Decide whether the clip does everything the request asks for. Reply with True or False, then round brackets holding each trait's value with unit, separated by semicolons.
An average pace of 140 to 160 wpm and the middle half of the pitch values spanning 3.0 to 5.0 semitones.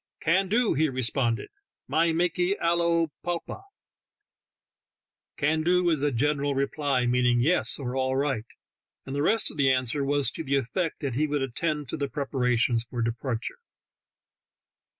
True (155 wpm; 4.2 semitones)